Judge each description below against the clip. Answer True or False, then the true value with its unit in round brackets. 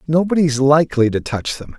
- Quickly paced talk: False (170 wpm)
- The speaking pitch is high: False (140 Hz)